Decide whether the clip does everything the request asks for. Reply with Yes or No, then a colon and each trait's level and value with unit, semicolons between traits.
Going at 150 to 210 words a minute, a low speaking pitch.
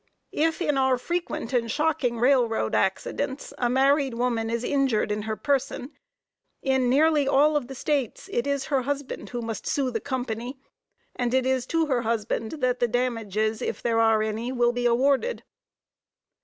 No: average, 170 wpm; very high, 250 Hz